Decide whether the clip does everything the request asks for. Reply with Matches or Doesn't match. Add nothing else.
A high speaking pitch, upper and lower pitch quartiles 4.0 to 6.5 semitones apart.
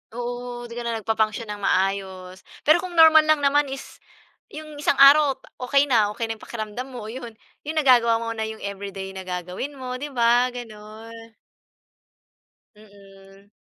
Matches